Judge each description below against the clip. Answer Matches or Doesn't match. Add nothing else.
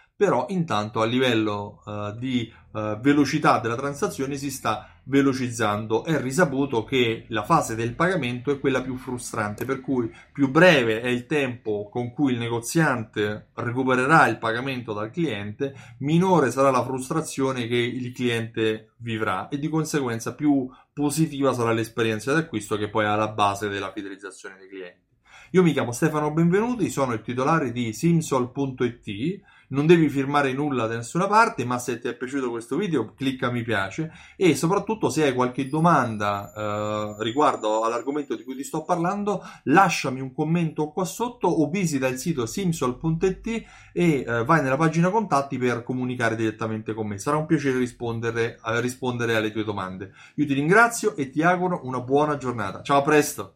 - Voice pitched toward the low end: Matches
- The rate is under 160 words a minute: Doesn't match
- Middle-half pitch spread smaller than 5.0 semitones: Doesn't match